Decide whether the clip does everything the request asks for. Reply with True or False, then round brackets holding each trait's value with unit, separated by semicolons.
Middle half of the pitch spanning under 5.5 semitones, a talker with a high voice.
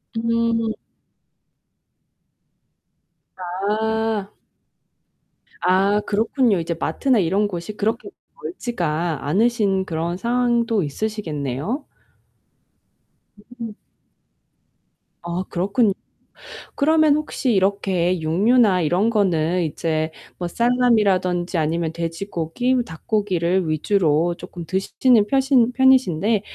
True (5.1 semitones; 195 Hz)